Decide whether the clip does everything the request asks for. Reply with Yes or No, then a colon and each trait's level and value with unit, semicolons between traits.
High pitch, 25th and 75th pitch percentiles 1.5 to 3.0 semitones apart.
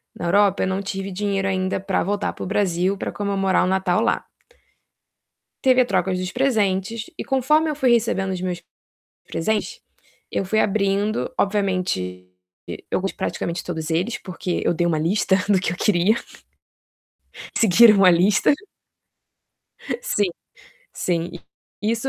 Yes: high, 195 Hz; average, 2.7 semitones